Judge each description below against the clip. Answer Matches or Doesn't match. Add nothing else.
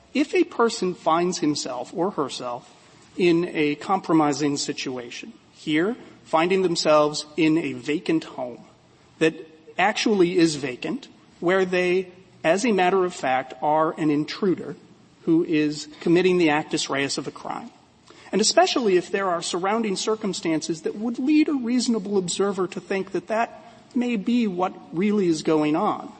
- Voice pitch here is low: Doesn't match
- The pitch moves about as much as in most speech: Matches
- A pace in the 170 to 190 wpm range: Doesn't match